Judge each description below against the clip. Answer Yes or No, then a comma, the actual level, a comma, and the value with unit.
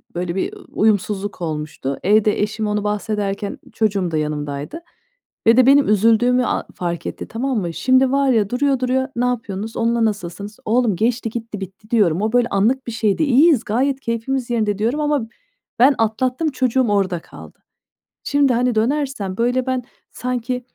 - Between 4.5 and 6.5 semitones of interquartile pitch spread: No, average, 3.9 semitones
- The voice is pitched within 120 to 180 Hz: No, high, 225 Hz